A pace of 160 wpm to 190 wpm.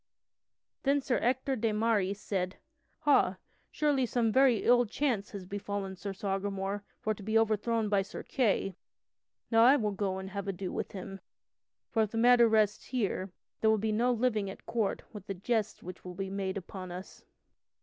Yes: average, 180 wpm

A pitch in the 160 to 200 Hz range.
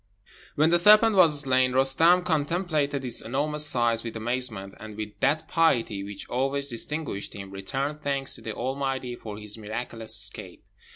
No: low, 130 Hz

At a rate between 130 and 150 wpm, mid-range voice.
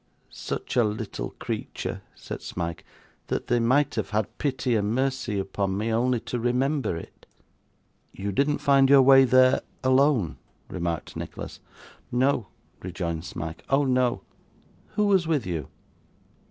No: average, 140 wpm; low, 120 Hz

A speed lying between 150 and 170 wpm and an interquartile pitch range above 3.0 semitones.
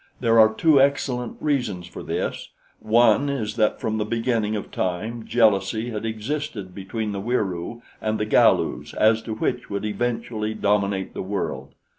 No: average, 160 wpm; narrow, 2.5 semitones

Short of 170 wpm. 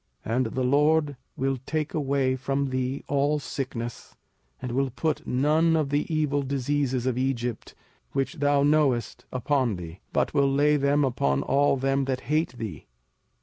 Yes: average, 160 wpm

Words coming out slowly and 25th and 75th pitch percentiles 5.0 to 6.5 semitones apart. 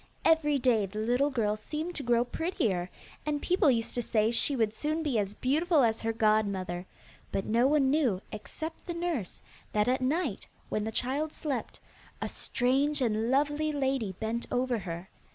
No: average, 175 wpm; wide, 5.5 semitones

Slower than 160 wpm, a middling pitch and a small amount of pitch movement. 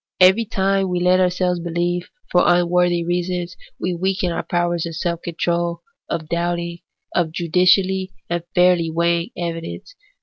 Yes: average, 140 wpm; medium, 175 Hz; narrow, 1.1 semitones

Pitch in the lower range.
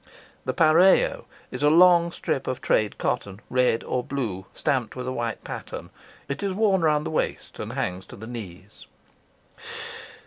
Yes: low, 130 Hz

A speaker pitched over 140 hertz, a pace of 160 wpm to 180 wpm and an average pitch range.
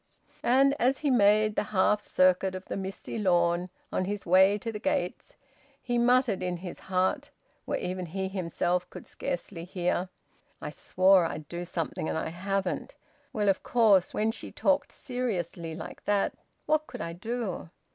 Yes: high, 190 Hz; average, 165 wpm; average, 3.6 semitones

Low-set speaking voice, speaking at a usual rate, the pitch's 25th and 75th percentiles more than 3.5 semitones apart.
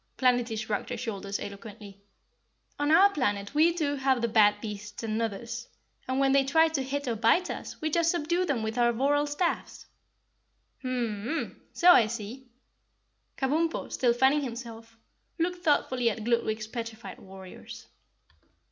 No: high, 245 Hz; average, 155 wpm; average, 4.9 semitones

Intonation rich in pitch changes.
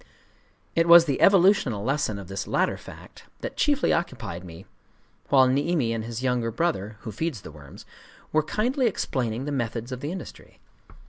Yes: wide, 7.1 semitones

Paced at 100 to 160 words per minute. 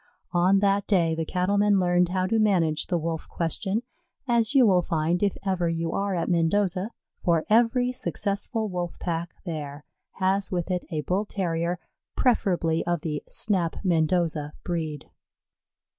Yes: average, 150 wpm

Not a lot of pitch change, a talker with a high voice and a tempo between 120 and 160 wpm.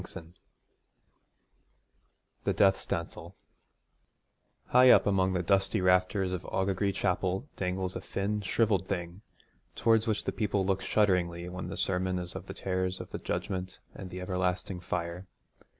No: narrow, 1.4 semitones; very low, 95 Hz; average, 145 wpm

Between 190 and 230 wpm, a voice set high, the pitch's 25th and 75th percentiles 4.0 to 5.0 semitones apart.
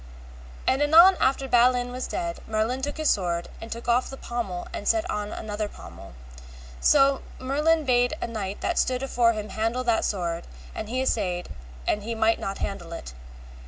No: average, 180 wpm; high, 235 Hz; average, 4.3 semitones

